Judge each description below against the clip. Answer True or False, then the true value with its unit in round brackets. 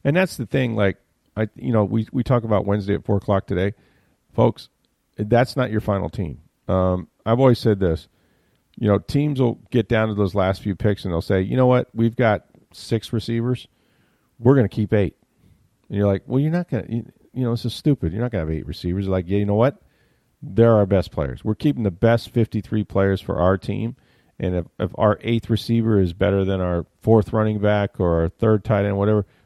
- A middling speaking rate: False (225 wpm)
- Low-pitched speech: True (105 Hz)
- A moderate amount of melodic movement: True (3.2 semitones)